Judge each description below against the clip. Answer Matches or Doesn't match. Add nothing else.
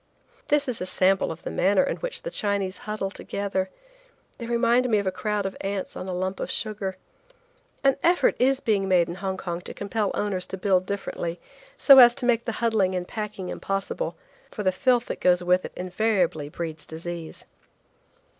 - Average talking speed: Matches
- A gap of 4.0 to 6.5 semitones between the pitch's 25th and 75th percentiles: Doesn't match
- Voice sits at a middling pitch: Doesn't match